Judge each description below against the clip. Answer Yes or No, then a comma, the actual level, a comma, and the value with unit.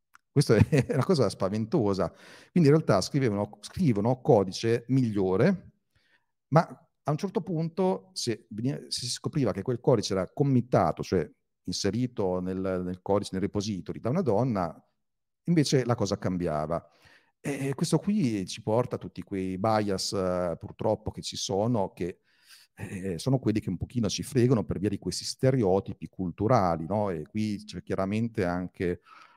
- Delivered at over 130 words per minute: Yes, average, 150 wpm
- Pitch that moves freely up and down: Yes, wide, 5.9 semitones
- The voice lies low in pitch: Yes, low, 105 Hz